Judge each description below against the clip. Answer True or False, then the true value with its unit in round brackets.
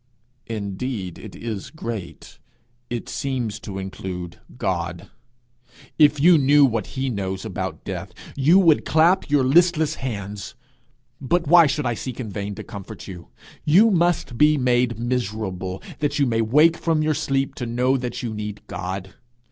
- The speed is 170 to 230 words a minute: False (155 wpm)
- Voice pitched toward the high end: False (120 Hz)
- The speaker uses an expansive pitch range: True (6.7 semitones)